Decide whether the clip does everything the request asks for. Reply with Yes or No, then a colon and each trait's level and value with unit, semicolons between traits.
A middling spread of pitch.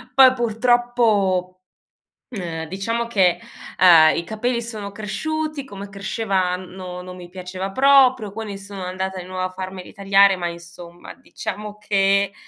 Yes: average, 3.6 semitones